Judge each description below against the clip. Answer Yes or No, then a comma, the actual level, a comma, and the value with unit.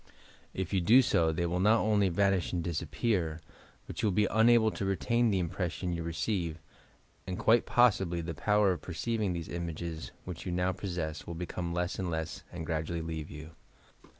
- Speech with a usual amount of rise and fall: Yes, average, 3.4 semitones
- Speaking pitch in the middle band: No, very low, 90 Hz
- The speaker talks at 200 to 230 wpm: No, average, 185 wpm